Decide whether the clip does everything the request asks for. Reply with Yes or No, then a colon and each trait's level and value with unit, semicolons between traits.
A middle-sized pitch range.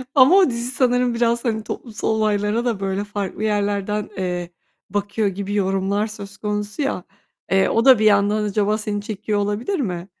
No: narrow, 2.3 semitones